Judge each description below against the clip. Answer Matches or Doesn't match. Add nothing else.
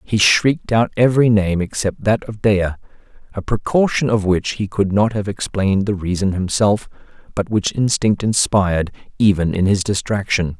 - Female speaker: Doesn't match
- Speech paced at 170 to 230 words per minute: Doesn't match